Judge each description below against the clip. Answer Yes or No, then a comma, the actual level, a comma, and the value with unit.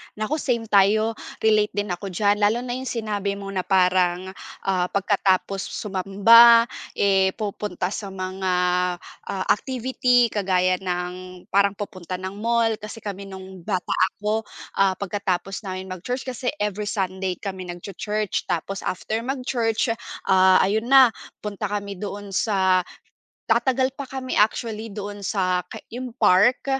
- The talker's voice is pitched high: Yes, high, 200 Hz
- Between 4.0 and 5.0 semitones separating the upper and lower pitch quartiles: No, average, 2.9 semitones